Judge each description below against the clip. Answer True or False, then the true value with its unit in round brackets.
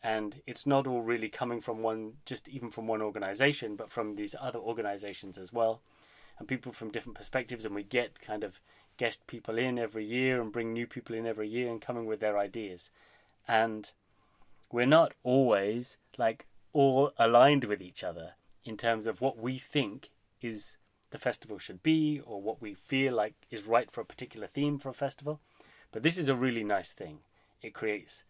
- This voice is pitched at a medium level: False (115 Hz)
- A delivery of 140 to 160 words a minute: False (195 wpm)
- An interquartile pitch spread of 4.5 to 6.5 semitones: False (3.3 semitones)